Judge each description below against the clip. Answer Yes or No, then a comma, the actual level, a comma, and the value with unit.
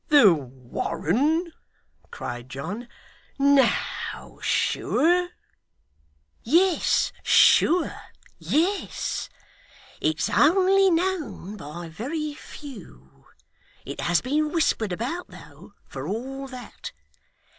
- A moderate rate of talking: No, slow, 80 wpm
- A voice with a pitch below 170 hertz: No, very high, 270 Hz